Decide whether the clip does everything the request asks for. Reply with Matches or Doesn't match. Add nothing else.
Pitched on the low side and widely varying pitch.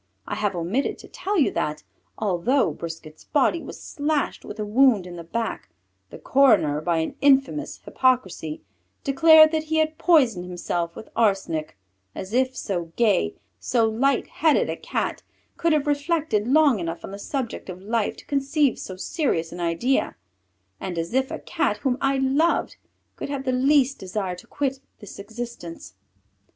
Doesn't match